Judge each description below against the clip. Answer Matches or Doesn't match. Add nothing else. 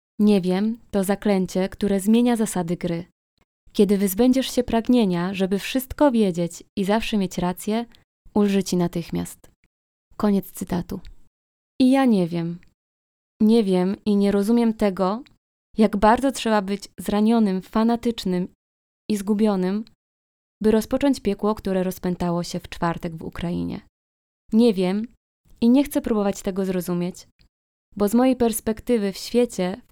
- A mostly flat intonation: Doesn't match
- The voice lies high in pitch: Matches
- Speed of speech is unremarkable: Matches